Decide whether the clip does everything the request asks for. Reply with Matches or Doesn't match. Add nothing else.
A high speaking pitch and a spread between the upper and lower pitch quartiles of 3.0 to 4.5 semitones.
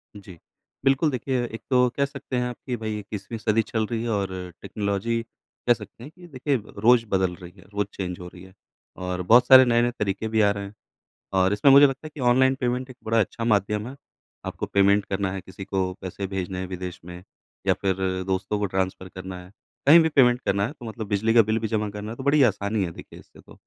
Doesn't match